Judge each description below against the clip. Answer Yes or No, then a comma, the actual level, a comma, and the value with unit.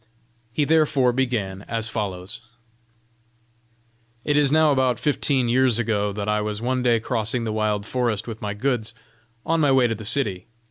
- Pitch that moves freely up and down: No, average, 3.7 semitones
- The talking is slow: No, average, 170 wpm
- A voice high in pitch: No, low, 115 Hz